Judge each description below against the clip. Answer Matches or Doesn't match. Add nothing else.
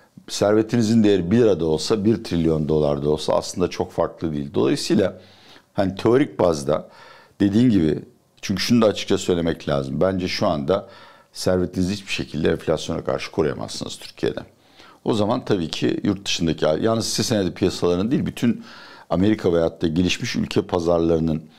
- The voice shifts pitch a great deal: Doesn't match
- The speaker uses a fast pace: Matches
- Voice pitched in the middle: Doesn't match